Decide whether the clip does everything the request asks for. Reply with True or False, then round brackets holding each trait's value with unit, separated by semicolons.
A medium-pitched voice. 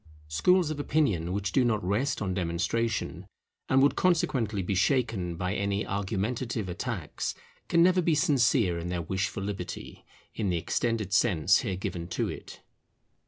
False (100 Hz)